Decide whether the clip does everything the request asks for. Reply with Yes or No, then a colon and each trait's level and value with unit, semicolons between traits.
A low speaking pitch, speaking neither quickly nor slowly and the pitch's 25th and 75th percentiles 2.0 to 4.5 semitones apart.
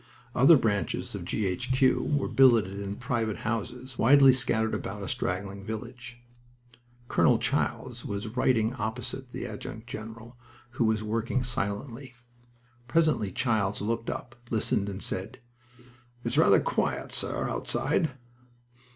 No: low, 115 Hz; slow, 130 wpm; average, 3.1 semitones